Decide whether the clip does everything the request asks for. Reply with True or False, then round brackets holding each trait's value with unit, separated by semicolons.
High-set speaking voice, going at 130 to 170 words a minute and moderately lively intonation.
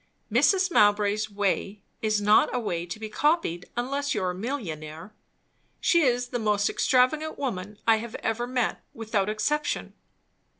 True (220 Hz; 145 wpm; 3.8 semitones)